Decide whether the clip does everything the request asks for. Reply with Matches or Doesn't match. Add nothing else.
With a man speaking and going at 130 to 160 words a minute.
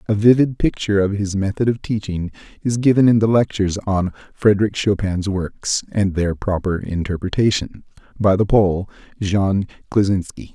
Matches